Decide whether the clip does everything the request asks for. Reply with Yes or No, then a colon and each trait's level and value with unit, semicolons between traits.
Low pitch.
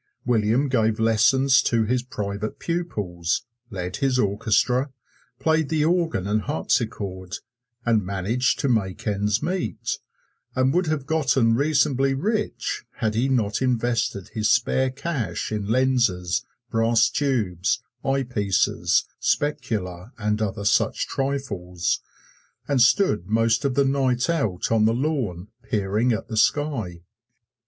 Yes: low, 115 Hz